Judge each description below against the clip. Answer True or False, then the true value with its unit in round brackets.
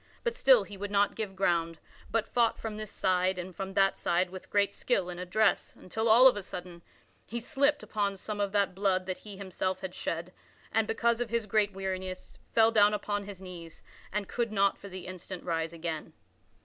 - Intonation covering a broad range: False (2.6 semitones)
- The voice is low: False (195 Hz)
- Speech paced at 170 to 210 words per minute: True (200 wpm)